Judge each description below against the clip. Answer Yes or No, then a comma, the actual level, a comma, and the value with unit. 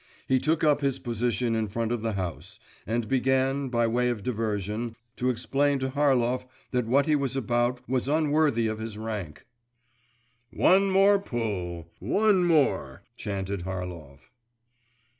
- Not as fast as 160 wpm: Yes, average, 145 wpm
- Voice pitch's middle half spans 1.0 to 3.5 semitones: No, average, 4.4 semitones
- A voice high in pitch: No, low, 120 Hz